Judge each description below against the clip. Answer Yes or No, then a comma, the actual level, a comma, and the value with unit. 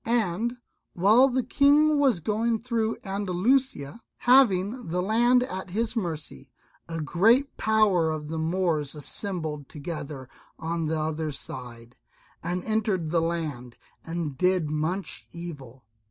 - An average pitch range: No, wide, 6.3 semitones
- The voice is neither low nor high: Yes, medium, 180 Hz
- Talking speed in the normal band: No, slow, 125 wpm